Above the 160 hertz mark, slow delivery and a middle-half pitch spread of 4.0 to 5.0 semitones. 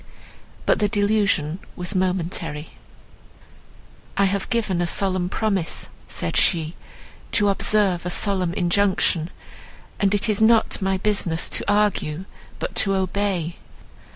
No: high, 190 Hz; slow, 125 wpm; average, 2.7 semitones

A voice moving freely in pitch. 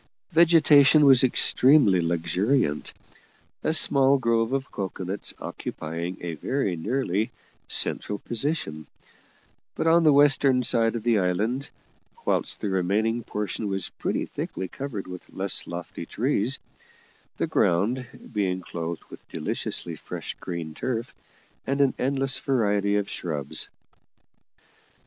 Yes: wide, 6.8 semitones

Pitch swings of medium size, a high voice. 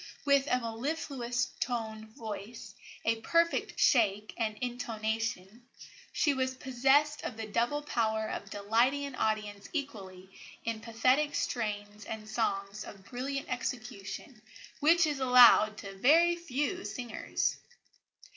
Yes: average, 4.0 semitones; high, 235 Hz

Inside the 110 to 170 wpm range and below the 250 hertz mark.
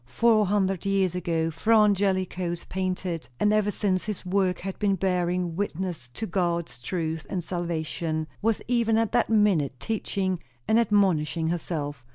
Yes: average, 150 wpm; medium, 185 Hz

